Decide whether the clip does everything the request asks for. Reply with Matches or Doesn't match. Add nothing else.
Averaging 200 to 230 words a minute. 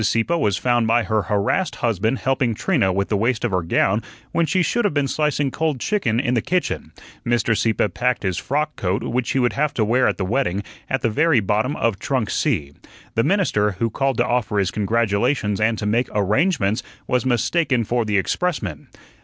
Matches